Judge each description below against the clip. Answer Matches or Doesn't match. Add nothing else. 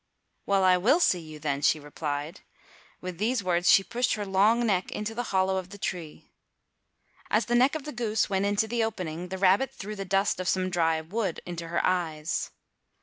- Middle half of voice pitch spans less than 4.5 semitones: Matches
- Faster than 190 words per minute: Matches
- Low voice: Doesn't match